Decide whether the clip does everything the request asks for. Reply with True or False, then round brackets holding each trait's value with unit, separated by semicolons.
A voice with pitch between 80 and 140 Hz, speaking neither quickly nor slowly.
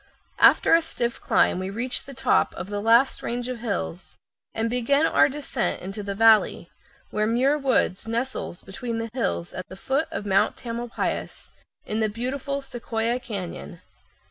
False (230 Hz; 165 wpm)